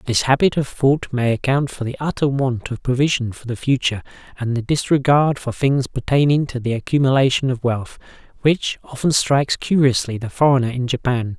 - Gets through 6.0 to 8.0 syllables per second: No, 5.4 syllables/s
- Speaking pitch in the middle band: No, low, 130 Hz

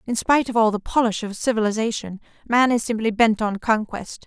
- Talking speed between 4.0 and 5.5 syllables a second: No, 5.7 syllables/s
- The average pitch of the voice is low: No, high, 225 Hz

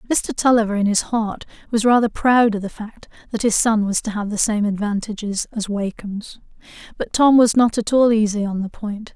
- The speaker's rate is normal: No, fast, 210 wpm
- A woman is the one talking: Yes, female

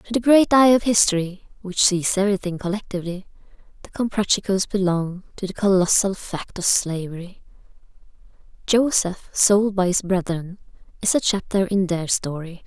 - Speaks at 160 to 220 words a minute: No, average, 140 wpm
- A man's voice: No, female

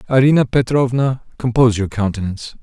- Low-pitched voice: Yes, low, 120 Hz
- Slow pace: Yes, slow, 115 wpm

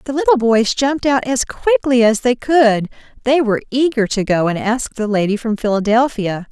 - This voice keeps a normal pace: Yes, average, 195 wpm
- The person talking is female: Yes, female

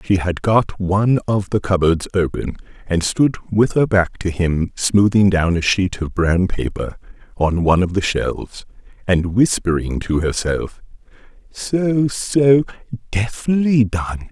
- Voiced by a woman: No, male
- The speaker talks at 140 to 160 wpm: Yes, average, 145 wpm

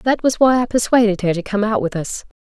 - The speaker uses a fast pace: Yes, fast, 270 wpm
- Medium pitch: No, high, 220 Hz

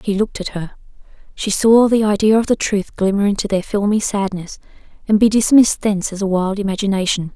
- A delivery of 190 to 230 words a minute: Yes, average, 195 wpm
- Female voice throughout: Yes, female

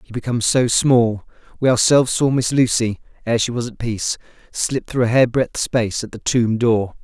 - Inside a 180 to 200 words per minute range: Yes, average, 190 wpm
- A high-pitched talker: No, low, 120 Hz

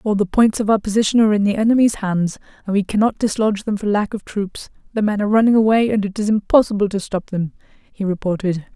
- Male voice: No, female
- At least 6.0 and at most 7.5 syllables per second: Yes, 6.4 syllables/s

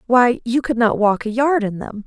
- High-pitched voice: Yes, high, 235 Hz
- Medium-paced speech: No, fast, 260 wpm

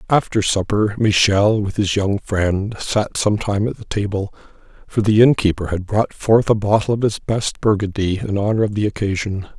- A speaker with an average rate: Yes, average, 190 wpm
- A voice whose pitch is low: Yes, low, 105 Hz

